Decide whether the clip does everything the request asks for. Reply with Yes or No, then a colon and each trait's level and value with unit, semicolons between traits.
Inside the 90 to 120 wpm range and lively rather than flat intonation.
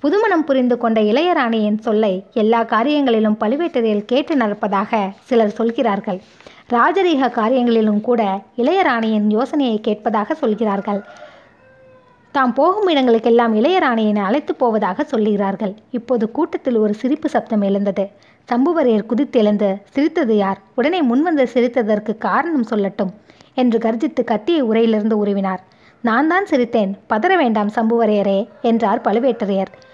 No: average, 110 wpm; average, 3.7 semitones